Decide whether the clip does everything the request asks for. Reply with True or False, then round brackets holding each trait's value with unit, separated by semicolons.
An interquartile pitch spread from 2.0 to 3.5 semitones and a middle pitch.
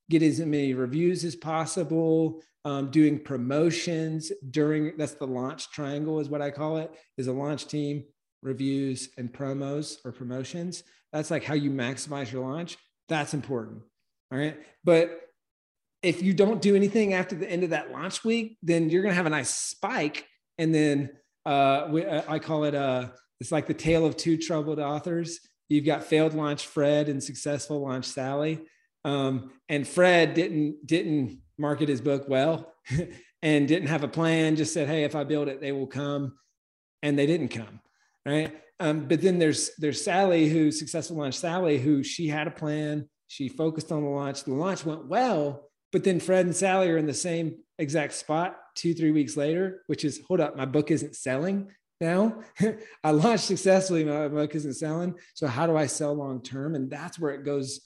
True (2.6 semitones; 150 Hz)